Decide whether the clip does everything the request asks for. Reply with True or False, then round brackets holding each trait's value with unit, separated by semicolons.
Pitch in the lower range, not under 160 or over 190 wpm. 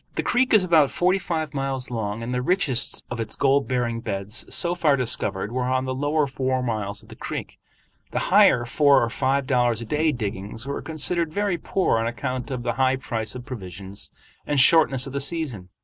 False (130 Hz; 205 wpm)